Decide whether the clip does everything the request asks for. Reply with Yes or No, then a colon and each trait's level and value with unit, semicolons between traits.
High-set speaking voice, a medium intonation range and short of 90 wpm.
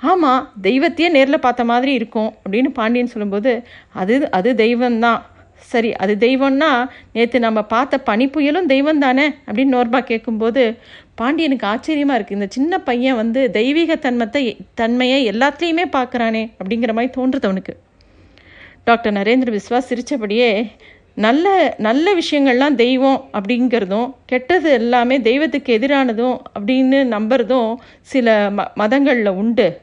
No: high, 245 Hz; average, 3.2 semitones; average, 120 wpm